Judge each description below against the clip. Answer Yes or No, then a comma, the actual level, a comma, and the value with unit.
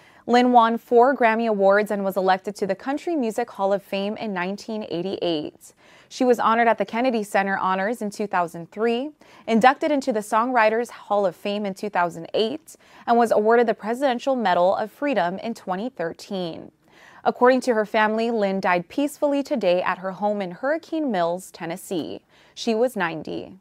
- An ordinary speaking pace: Yes, average, 165 wpm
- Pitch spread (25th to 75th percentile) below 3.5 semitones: No, average, 4.0 semitones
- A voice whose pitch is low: No, high, 215 Hz